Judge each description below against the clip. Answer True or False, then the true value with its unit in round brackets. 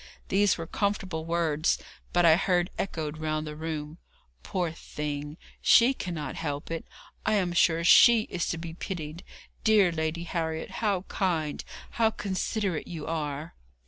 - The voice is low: False (165 Hz)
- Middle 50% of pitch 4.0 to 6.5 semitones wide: False (3.1 semitones)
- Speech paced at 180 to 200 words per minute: False (145 wpm)